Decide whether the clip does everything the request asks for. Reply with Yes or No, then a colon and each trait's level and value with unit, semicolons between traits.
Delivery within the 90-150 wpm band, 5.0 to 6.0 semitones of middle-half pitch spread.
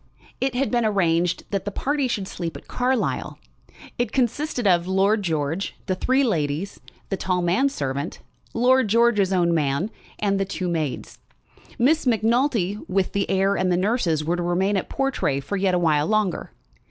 No: average, 175 wpm; average, 5.3 semitones